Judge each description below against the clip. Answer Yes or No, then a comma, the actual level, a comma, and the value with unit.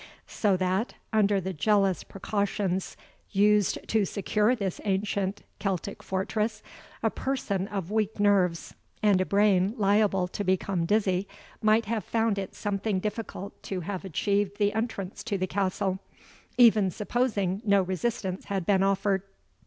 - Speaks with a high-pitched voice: Yes, high, 200 Hz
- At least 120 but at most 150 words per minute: Yes, average, 140 wpm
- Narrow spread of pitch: Yes, narrow, 1.9 semitones